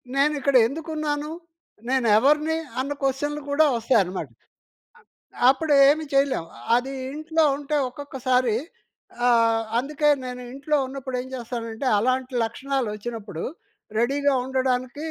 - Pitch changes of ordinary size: Yes, average, 3.3 semitones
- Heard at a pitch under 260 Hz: No, very high, 265 Hz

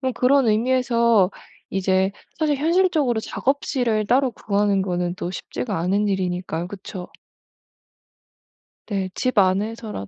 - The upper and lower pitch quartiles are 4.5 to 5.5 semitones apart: Yes, average, 5.2 semitones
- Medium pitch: No, high, 210 Hz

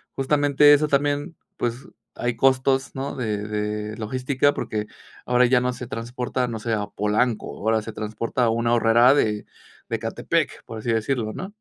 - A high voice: No, low, 120 Hz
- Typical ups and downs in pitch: Yes, average, 3.5 semitones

